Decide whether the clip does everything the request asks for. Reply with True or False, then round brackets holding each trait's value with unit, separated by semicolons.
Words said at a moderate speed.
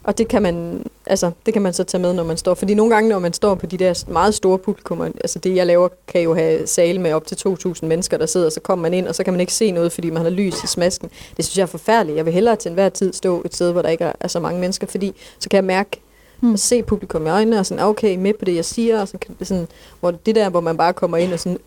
False (305 wpm)